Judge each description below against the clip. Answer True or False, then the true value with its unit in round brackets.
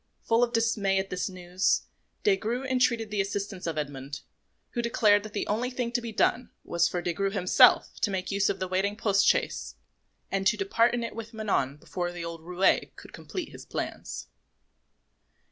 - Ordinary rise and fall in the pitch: True (4.2 semitones)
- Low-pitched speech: False (200 Hz)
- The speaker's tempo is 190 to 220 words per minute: True (195 wpm)